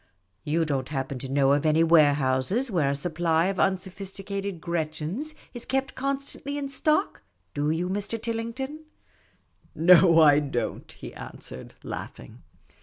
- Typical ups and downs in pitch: No, wide, 7.5 semitones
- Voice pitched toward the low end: No, medium, 175 Hz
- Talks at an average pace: Yes, average, 145 wpm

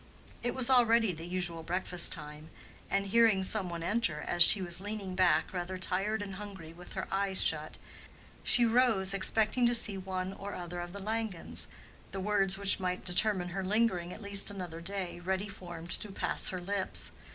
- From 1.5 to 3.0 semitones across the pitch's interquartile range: Yes, average, 2.7 semitones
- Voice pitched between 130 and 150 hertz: No, high, 190 Hz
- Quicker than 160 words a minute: Yes, average, 180 wpm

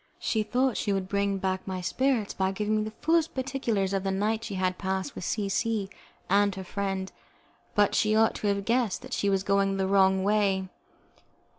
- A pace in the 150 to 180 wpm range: No, average, 200 wpm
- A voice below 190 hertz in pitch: No, high, 200 Hz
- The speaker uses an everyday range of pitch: No, narrow, 2.1 semitones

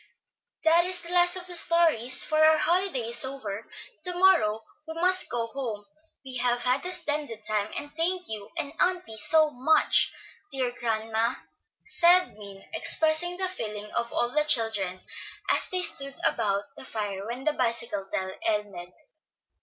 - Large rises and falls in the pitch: Yes, wide, 7.5 semitones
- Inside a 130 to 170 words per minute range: Yes, average, 165 wpm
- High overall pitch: Yes, very high, 255 Hz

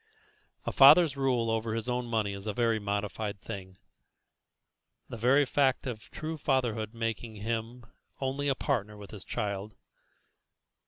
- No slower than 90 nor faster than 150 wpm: Yes, average, 145 wpm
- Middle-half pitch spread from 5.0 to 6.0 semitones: No, average, 3.8 semitones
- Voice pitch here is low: Yes, low, 115 Hz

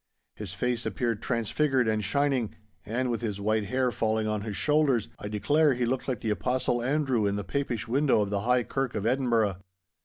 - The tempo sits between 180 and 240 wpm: Yes, average, 195 wpm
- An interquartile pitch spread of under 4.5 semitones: Yes, average, 3.5 semitones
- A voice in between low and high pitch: No, low, 120 Hz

